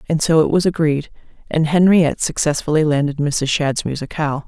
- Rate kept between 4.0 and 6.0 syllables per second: Yes, 5.6 syllables/s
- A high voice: No, medium, 155 Hz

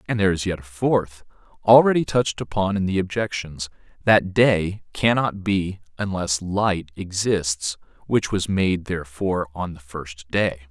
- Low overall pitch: Yes, very low, 95 Hz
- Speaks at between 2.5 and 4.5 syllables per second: Yes, 4.4 syllables/s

